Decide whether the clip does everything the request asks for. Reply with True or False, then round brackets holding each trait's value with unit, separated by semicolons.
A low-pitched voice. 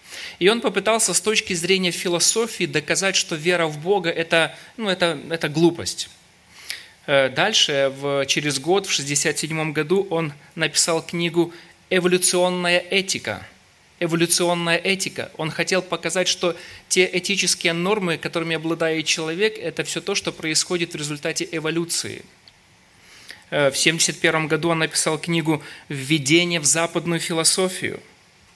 False (170 Hz)